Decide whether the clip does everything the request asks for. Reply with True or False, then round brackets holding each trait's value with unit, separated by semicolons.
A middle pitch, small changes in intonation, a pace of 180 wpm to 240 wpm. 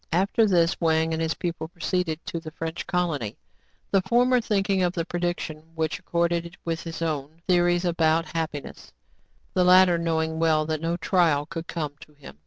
True (165 Hz; 1.8 semitones; 185 wpm)